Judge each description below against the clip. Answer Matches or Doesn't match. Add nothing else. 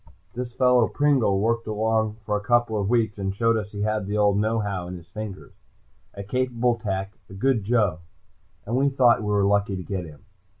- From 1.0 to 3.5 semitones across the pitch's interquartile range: Matches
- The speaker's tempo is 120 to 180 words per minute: Doesn't match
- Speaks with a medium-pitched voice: Doesn't match